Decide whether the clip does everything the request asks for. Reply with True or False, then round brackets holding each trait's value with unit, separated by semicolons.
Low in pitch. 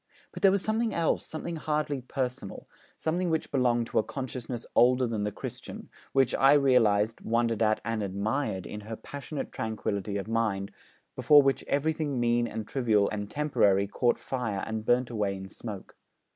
True (120 Hz)